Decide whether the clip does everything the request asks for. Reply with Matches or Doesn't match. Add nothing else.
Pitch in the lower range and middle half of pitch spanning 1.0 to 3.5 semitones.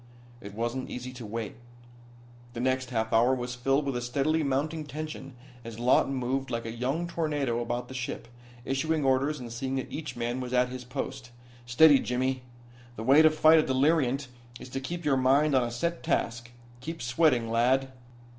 Matches